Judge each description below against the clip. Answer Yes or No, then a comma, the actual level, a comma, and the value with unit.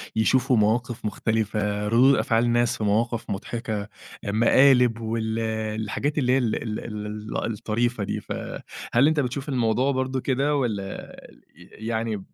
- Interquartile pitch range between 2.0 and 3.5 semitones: Yes, average, 2.9 semitones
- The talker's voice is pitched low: Yes, low, 115 Hz